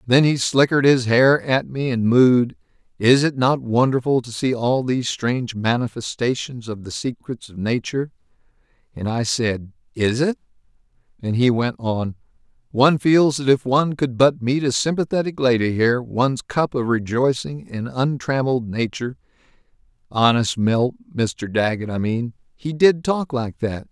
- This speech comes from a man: Yes, male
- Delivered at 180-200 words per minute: No, average, 160 wpm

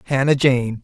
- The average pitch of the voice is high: No, low, 130 Hz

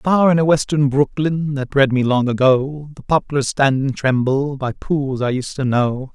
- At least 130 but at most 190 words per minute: No, fast, 205 wpm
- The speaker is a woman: No, male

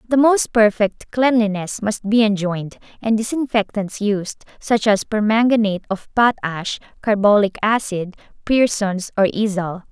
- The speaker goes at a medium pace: No, slow, 120 wpm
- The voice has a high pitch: Yes, high, 210 Hz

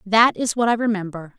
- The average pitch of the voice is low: No, high, 215 Hz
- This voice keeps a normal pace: No, fast, 215 wpm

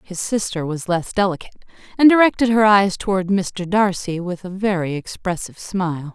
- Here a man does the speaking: No, female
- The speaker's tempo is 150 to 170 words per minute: Yes, average, 165 wpm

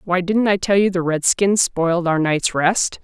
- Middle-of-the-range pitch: Yes, medium, 180 Hz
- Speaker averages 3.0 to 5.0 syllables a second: Yes, 4.5 syllables/s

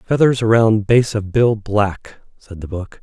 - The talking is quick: No, average, 180 wpm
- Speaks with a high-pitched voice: No, low, 105 Hz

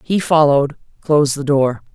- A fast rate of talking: No, average, 155 wpm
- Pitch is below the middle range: No, medium, 145 Hz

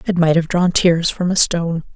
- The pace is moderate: No, fast, 245 wpm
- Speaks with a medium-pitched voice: Yes, medium, 170 Hz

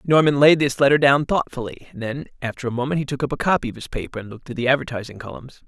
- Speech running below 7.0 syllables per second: No, 7.2 syllables/s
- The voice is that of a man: Yes, male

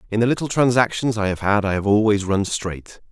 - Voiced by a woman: No, male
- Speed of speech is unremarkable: No, fast, 230 wpm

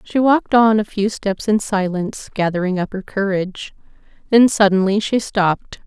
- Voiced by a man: No, female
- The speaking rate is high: No, average, 165 wpm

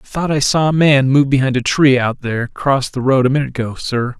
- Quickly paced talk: Yes, fast, 270 wpm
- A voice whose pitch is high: No, low, 135 Hz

